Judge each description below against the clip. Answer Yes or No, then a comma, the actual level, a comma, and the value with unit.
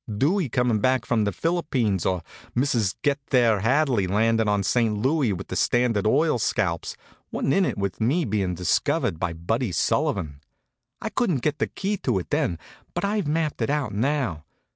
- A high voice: No, low, 115 Hz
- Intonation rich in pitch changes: Yes, wide, 6.6 semitones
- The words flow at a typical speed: Yes, average, 180 wpm